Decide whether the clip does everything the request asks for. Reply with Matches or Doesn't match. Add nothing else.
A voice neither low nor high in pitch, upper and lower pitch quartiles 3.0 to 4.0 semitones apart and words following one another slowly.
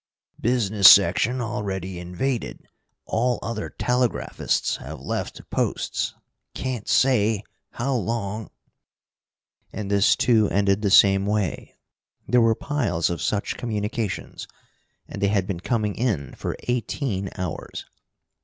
Doesn't match